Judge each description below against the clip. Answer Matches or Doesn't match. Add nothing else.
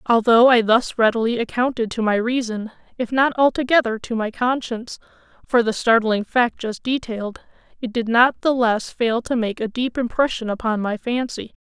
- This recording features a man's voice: Doesn't match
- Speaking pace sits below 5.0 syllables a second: Doesn't match